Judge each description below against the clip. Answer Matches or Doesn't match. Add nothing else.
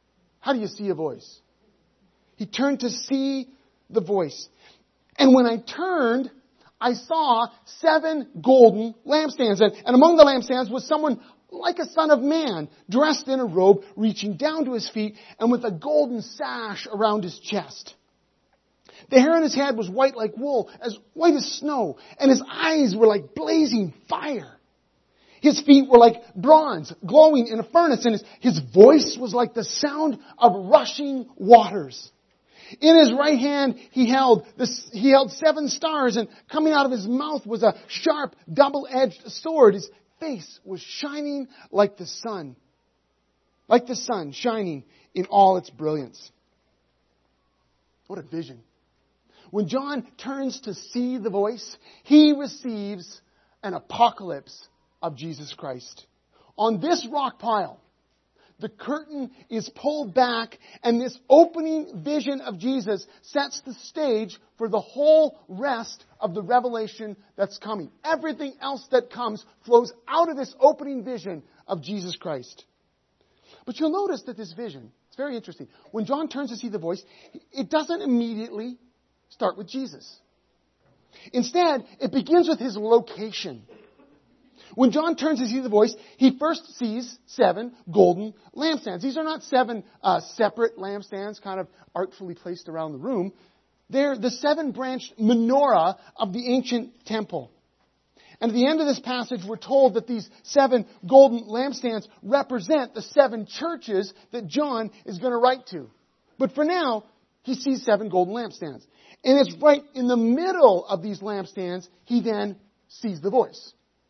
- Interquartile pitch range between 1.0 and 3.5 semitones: Doesn't match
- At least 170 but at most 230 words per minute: Doesn't match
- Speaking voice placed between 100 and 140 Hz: Doesn't match